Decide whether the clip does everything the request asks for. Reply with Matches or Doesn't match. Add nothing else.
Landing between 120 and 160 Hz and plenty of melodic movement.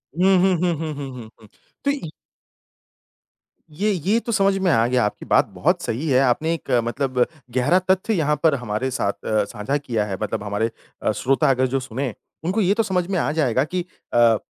Matches